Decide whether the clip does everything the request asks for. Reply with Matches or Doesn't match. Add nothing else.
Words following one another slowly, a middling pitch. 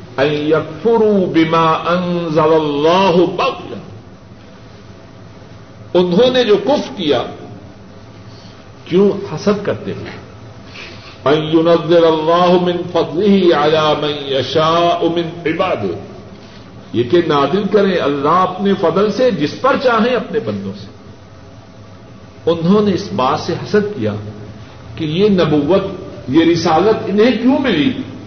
Matches